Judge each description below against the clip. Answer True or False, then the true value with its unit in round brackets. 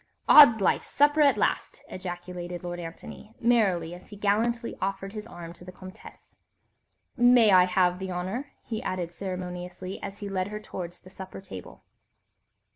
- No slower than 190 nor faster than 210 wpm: False (165 wpm)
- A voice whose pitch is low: False (190 Hz)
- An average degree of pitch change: True (3.2 semitones)